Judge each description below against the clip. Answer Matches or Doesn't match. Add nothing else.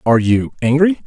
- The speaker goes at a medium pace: Matches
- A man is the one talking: Matches